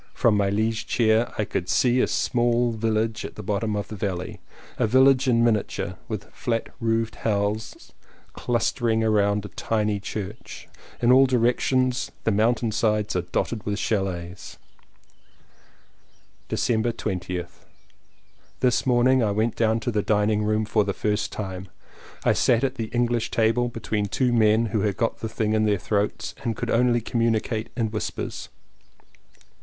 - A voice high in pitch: No, low, 110 Hz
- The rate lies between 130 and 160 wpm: Yes, average, 155 wpm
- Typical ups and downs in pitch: No, narrow, 2.3 semitones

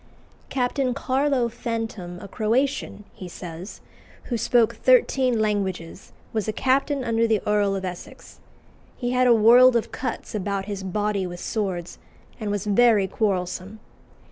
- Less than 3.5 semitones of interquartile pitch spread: No, average, 3.9 semitones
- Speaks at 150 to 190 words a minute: No, average, 140 wpm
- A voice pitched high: Yes, high, 215 Hz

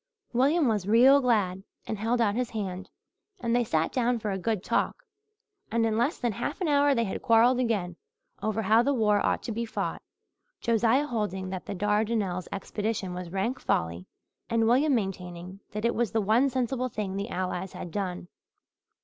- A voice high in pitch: Yes, high, 220 Hz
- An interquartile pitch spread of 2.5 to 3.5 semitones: No, average, 3.9 semitones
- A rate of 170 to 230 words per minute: Yes, average, 185 wpm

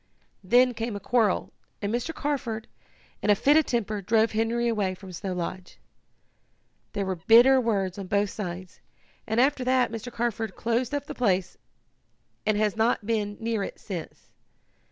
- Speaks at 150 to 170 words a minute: Yes, average, 165 wpm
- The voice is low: No, high, 220 Hz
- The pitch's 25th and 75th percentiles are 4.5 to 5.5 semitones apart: No, average, 3.1 semitones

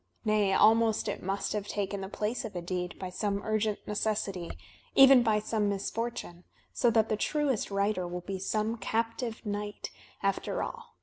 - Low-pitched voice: No, high, 210 Hz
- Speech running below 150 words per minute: No, average, 170 wpm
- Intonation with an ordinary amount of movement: No, narrow, 2.2 semitones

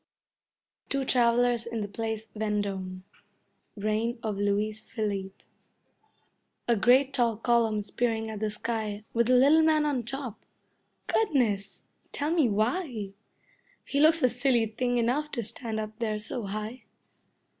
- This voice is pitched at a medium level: No, high, 230 Hz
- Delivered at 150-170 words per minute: No, slow, 135 wpm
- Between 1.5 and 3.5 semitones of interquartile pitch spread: Yes, average, 3.0 semitones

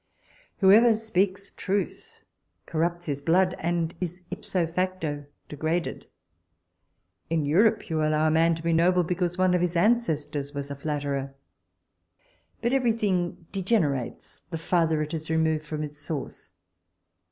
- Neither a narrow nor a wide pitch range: Yes, average, 3.4 semitones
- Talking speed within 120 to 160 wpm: Yes, average, 140 wpm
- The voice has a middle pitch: Yes, medium, 170 Hz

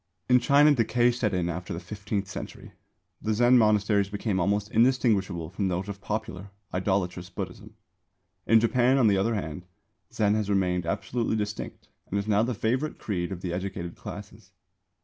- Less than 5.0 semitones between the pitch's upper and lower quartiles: Yes, average, 3.3 semitones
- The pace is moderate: Yes, average, 170 wpm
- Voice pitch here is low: Yes, low, 105 Hz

